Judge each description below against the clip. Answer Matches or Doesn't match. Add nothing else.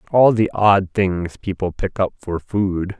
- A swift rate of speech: Doesn't match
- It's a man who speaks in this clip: Matches